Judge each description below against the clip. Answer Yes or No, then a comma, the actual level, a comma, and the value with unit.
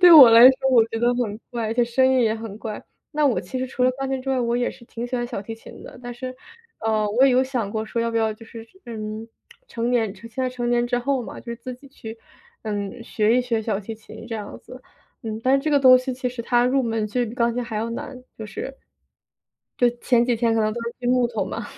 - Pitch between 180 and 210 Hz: No, high, 240 Hz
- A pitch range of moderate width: No, narrow, 2.2 semitones